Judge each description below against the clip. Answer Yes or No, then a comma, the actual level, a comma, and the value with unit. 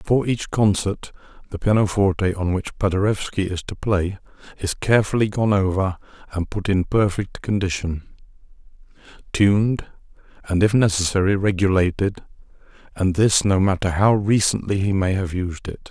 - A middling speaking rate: No, slow, 130 wpm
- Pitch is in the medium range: No, low, 100 Hz